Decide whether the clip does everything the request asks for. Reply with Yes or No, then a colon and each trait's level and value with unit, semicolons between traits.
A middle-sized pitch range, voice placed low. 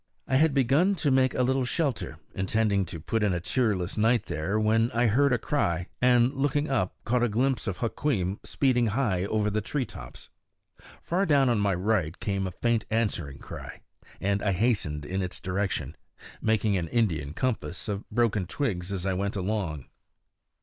Yes: average, 4.9 semitones; low, 110 Hz